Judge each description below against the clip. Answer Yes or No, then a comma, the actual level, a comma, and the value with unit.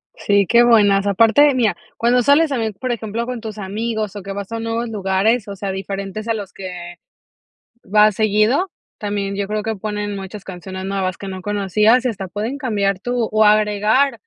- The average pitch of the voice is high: Yes, high, 210 Hz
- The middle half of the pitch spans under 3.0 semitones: Yes, narrow, 2.5 semitones